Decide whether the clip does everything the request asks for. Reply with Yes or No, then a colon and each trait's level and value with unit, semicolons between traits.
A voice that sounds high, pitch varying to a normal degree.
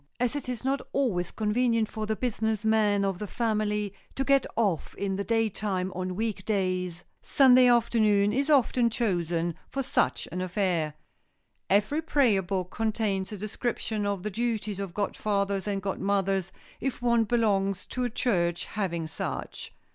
Yes: high, 210 Hz; average, 3.3 semitones